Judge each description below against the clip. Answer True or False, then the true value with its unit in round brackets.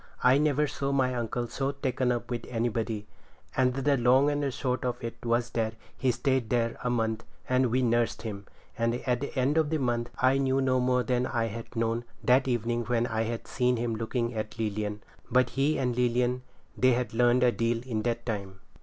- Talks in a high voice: False (120 Hz)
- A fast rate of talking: True (210 wpm)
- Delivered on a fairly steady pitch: True (1.8 semitones)